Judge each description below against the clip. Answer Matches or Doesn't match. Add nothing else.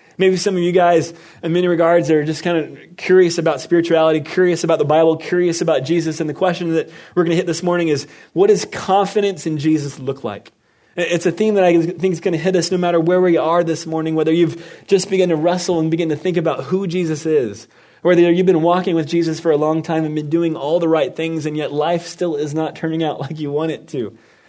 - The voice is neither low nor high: Matches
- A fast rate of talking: Matches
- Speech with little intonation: Matches